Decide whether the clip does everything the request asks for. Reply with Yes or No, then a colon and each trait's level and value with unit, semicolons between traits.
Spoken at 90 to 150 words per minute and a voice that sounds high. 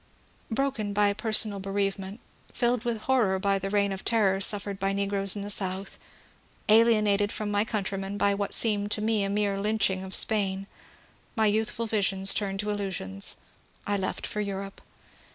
No: average, 170 wpm; high, 200 Hz